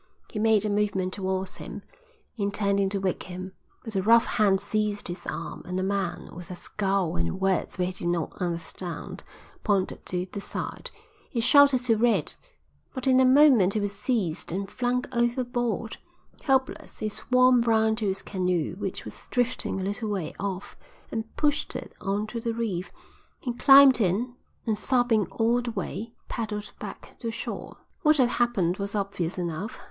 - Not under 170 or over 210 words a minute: Yes, average, 175 wpm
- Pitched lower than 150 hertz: No, high, 210 Hz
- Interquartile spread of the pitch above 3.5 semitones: Yes, average, 4.1 semitones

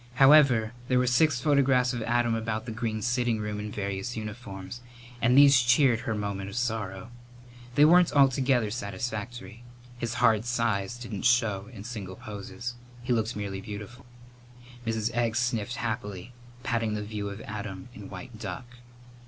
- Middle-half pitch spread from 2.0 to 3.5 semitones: Yes, average, 2.9 semitones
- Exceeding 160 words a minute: No, average, 155 wpm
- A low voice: Yes, low, 115 Hz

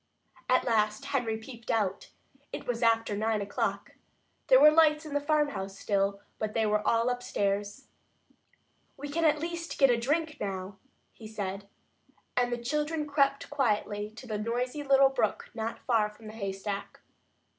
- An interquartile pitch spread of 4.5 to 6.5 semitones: Yes, average, 5.1 semitones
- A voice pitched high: Yes, high, 230 Hz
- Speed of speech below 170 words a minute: Yes, average, 160 wpm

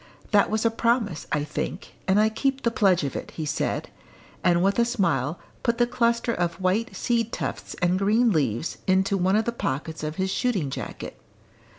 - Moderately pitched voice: No, high, 195 Hz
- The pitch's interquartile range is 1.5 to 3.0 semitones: No, wide, 5.4 semitones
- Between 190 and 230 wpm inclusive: Yes, average, 195 wpm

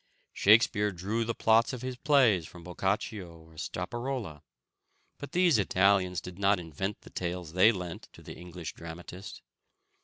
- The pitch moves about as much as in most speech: Yes, average, 4.5 semitones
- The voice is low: Yes, very low, 95 Hz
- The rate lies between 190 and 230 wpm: No, average, 150 wpm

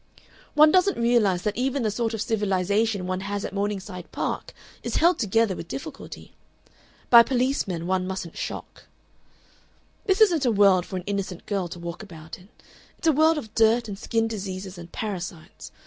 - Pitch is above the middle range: Yes, high, 205 Hz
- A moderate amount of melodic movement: Yes, average, 4.2 semitones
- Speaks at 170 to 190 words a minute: Yes, average, 175 wpm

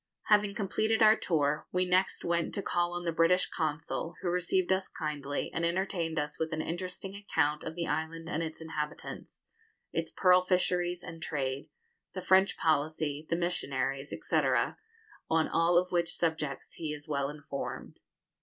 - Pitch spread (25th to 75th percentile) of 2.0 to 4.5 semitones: Yes, average, 3.0 semitones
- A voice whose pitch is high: No, medium, 165 Hz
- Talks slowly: No, average, 165 wpm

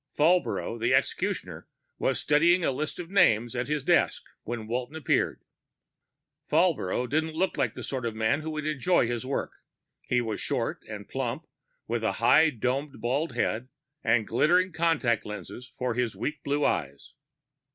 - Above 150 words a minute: Yes, average, 160 wpm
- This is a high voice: No, low, 130 Hz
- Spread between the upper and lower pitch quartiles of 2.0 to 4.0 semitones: No, average, 5.1 semitones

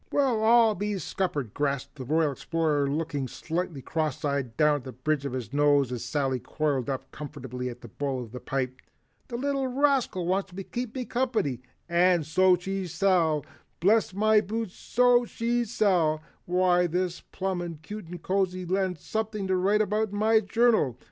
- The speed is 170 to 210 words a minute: Yes, average, 175 wpm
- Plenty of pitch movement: Yes, wide, 6.7 semitones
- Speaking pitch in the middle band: Yes, medium, 175 Hz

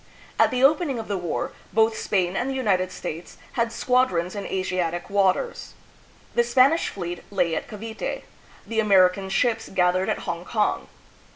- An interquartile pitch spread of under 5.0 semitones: Yes, average, 4.5 semitones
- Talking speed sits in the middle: Yes, average, 160 wpm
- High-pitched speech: Yes, high, 200 Hz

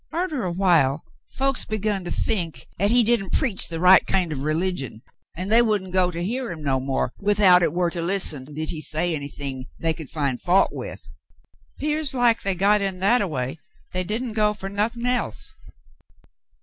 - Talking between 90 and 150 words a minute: No, average, 190 wpm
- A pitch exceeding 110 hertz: Yes, medium, 185 Hz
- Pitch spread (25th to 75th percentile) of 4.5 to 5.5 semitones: Yes, average, 5.1 semitones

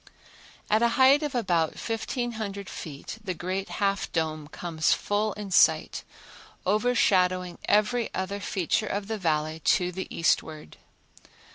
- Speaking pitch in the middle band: No, high, 195 Hz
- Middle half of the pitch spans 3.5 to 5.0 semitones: Yes, average, 4.0 semitones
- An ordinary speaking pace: No, slow, 130 wpm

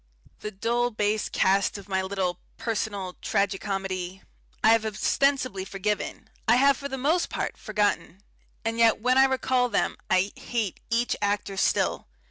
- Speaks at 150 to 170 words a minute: Yes, average, 155 wpm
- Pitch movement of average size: Yes, average, 3.8 semitones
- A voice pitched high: Yes, high, 210 Hz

